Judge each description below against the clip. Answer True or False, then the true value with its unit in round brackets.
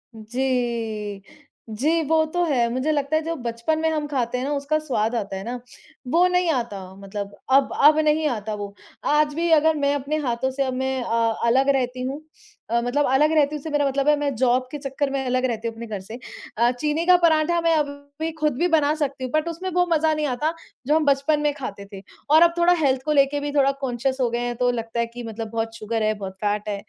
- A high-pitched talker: True (270 Hz)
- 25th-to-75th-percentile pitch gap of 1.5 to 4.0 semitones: False (4.5 semitones)